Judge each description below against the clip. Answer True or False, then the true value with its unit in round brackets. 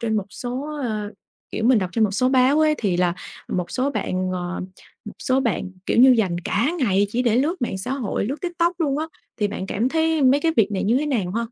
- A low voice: False (240 Hz)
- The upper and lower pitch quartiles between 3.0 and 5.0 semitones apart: False (5.6 semitones)